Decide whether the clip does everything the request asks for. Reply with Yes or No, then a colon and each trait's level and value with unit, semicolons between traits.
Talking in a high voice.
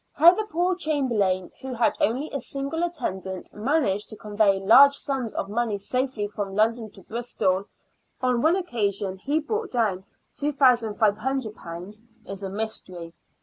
Yes: high, 230 Hz